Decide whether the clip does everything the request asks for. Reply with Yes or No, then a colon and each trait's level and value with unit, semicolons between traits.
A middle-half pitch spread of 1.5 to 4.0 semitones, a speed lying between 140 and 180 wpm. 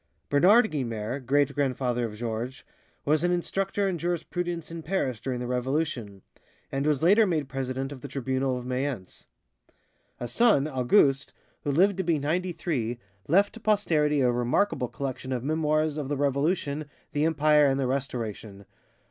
No: average, 4.4 semitones; average, 160 wpm